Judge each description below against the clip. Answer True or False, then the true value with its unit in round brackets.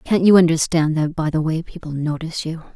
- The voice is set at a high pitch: False (160 Hz)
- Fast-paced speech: True (220 wpm)